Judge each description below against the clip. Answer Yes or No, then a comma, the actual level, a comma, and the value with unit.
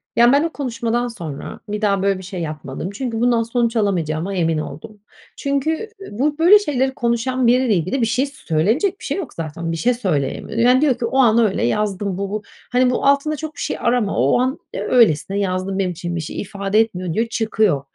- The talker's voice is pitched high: Yes, high, 225 Hz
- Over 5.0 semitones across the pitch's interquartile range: Yes, wide, 5.4 semitones